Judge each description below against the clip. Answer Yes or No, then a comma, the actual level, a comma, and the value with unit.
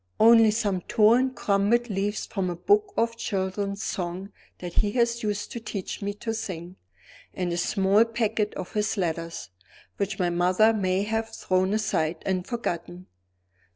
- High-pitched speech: Yes, high, 205 Hz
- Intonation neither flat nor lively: Yes, average, 3.3 semitones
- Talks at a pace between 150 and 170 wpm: Yes, average, 155 wpm